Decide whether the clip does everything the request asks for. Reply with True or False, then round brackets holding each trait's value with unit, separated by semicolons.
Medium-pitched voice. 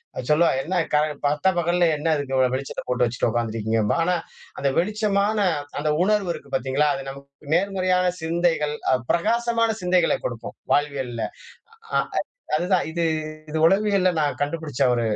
True (160 Hz)